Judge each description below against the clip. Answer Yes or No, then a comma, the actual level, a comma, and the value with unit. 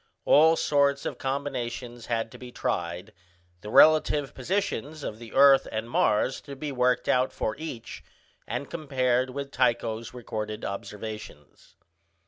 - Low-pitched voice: Yes, low, 125 Hz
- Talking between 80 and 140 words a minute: Yes, slow, 135 wpm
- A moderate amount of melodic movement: Yes, average, 3.9 semitones